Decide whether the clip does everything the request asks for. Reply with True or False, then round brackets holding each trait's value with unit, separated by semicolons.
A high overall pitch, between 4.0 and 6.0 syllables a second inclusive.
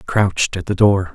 False (95 Hz; 5.0 syllables/s)